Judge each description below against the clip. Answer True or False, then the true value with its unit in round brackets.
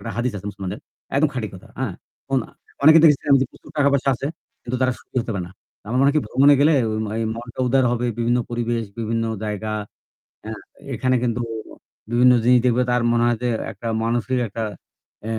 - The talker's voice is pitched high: False (120 Hz)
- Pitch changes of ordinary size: False (2.3 semitones)